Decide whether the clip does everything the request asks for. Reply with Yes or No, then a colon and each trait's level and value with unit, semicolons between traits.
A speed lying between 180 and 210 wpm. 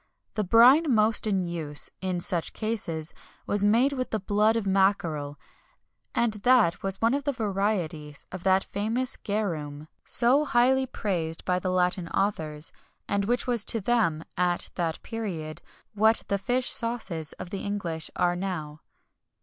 No: average, 155 wpm